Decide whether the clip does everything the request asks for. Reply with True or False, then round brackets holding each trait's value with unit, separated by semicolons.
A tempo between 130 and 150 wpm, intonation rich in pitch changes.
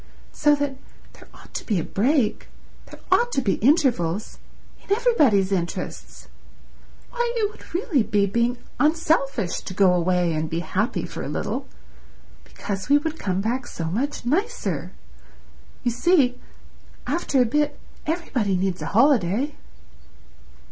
True (140 wpm; 7.6 semitones)